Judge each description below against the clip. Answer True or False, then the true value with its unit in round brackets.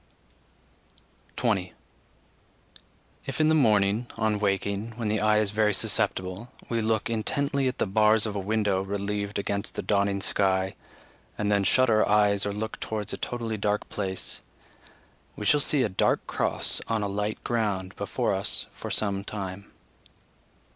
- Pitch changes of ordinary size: False (1.8 semitones)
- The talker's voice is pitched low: True (105 Hz)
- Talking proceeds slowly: False (155 wpm)